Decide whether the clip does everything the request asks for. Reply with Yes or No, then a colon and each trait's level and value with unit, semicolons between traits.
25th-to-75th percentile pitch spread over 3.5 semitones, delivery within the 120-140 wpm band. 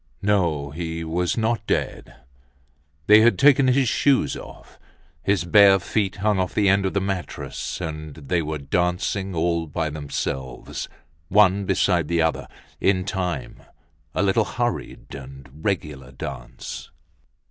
Yes: average, 4.5 semitones; slow, 135 wpm